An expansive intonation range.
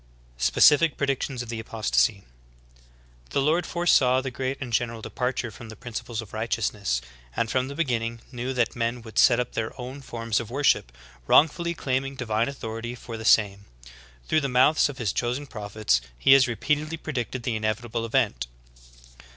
No: average, 3.3 semitones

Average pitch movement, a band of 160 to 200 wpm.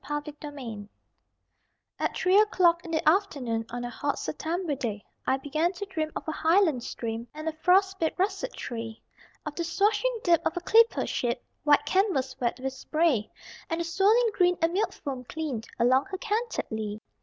No: wide, 6.7 semitones; average, 180 wpm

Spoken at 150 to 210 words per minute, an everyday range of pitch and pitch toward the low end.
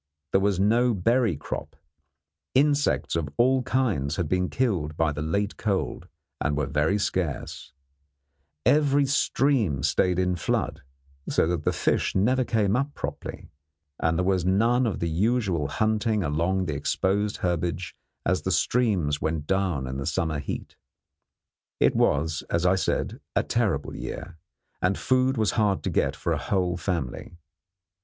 No: average, 155 wpm; wide, 5.7 semitones; very low, 95 Hz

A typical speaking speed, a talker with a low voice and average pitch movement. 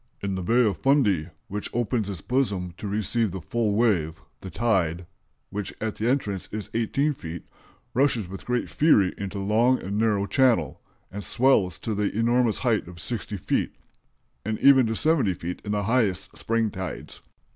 Yes: average, 180 wpm; low, 105 Hz; average, 3.9 semitones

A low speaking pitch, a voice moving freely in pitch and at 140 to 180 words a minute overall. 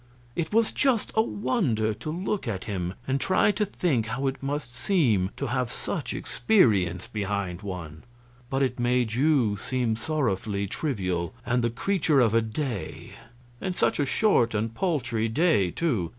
Yes: low, 120 Hz; wide, 6.9 semitones; average, 165 wpm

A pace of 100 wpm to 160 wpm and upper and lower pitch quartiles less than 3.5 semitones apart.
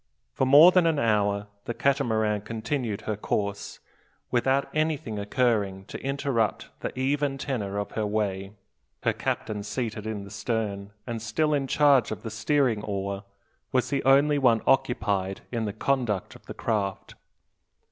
No: average, 155 wpm; average, 4.9 semitones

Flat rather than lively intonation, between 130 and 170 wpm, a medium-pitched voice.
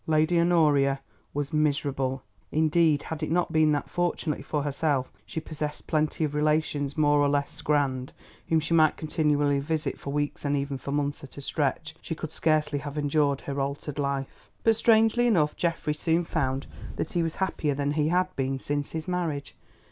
No: narrow, 2.2 semitones; average, 185 wpm; medium, 150 Hz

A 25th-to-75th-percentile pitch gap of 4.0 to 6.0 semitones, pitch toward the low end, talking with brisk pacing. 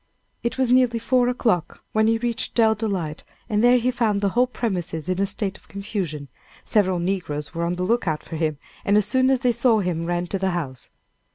No: average, 5.2 semitones; high, 200 Hz; fast, 215 wpm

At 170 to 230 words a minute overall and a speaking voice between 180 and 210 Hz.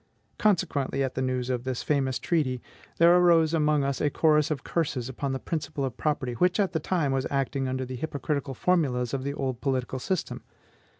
No: average, 195 wpm; medium, 140 Hz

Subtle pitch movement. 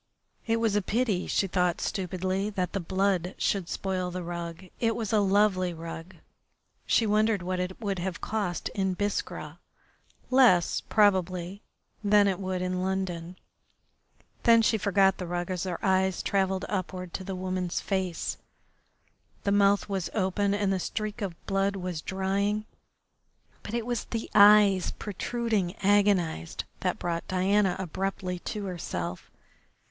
Yes: narrow, 2.1 semitones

